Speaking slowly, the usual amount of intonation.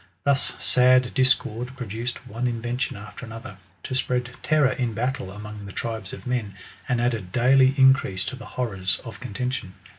No: average, 160 wpm; average, 3.1 semitones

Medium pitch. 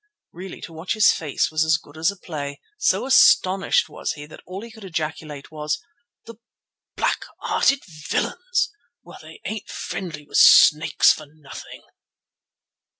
Yes: medium, 160 Hz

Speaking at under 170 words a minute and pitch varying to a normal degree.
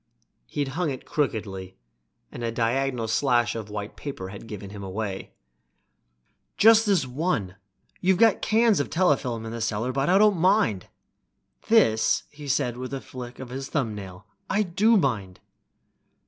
No: average, 150 wpm; wide, 7.7 semitones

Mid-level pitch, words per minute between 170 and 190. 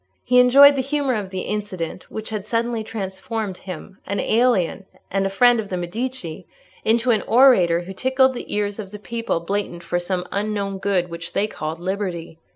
No: high, 205 Hz; average, 185 wpm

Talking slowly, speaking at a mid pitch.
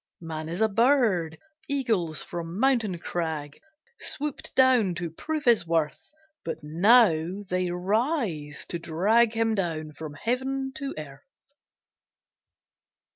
Yes: slow, 120 wpm; medium, 180 Hz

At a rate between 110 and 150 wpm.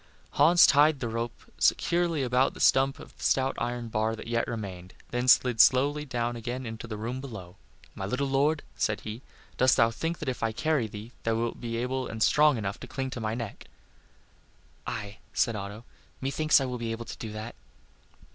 No: average, 200 wpm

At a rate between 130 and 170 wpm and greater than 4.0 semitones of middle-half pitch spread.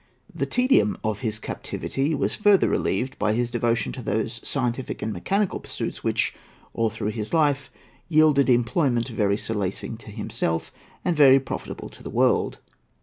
Yes: average, 150 wpm; average, 4.7 semitones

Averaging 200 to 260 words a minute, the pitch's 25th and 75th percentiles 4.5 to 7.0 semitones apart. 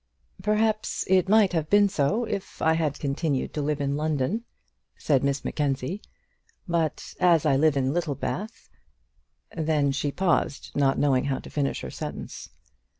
No: average, 155 wpm; average, 4.8 semitones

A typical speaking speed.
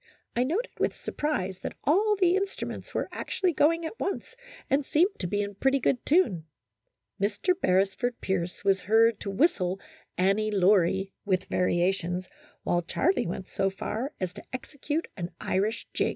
Yes: average, 165 wpm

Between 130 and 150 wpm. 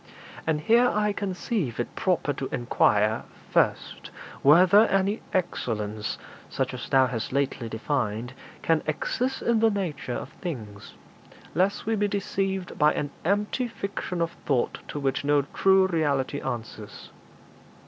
Yes: average, 140 wpm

